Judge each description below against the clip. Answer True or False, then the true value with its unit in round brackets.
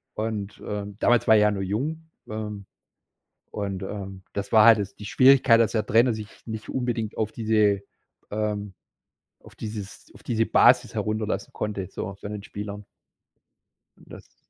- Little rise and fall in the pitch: True (1.7 semitones)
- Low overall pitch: True (105 Hz)